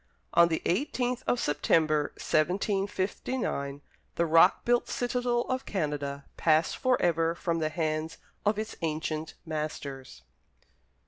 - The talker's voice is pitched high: No, medium, 165 Hz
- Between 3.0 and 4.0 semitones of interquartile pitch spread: No, wide, 5.4 semitones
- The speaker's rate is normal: No, slow, 120 wpm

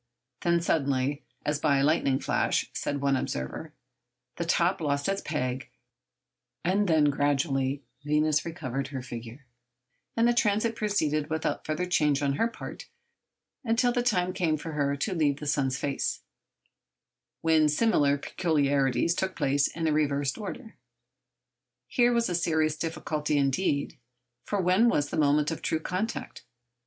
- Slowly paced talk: No, average, 145 wpm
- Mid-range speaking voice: Yes, medium, 150 Hz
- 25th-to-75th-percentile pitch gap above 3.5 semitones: Yes, average, 4.2 semitones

